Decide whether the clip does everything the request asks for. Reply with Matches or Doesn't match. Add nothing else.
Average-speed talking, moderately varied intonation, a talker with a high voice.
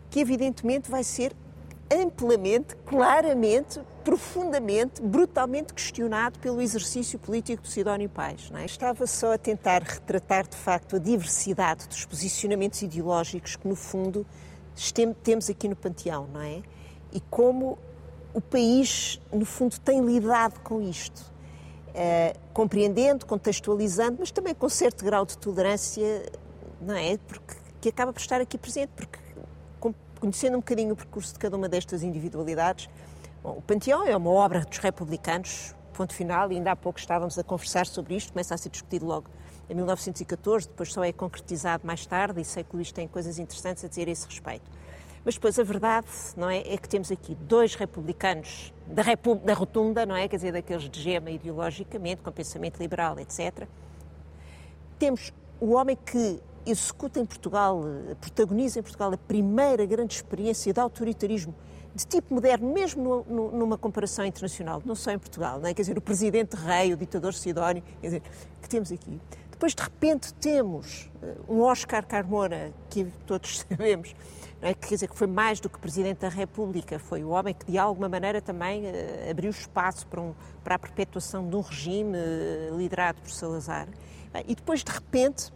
Matches